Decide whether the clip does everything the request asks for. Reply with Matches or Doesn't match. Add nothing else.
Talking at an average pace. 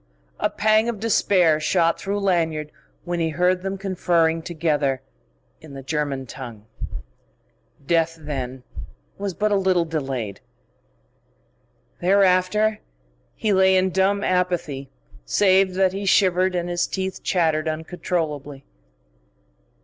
Doesn't match